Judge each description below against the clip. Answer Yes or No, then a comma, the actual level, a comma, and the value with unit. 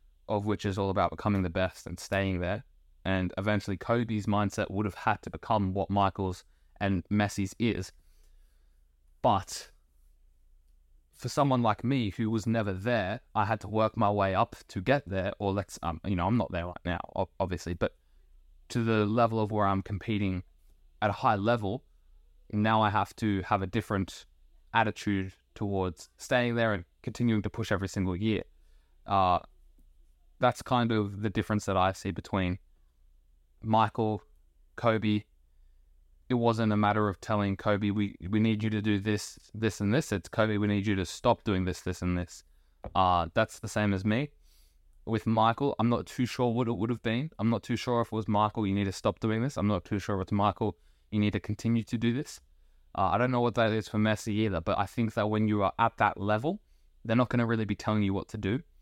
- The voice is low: Yes, low, 105 Hz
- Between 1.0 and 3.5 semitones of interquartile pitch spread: No, average, 3.9 semitones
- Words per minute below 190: No, fast, 205 wpm